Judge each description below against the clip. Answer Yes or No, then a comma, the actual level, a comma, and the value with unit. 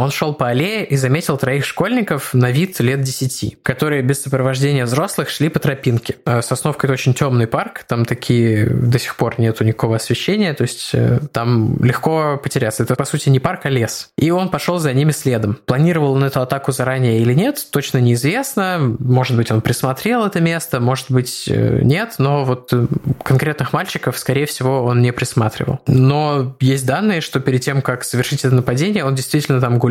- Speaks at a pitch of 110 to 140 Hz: Yes, low, 135 Hz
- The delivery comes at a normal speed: No, fast, 185 wpm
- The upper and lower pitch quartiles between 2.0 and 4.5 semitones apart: Yes, average, 3.3 semitones